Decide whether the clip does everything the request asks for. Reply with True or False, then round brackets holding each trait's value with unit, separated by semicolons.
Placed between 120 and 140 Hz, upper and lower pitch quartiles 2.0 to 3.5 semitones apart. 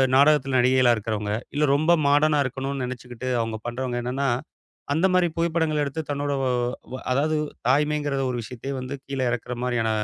True (135 Hz; 3.1 semitones)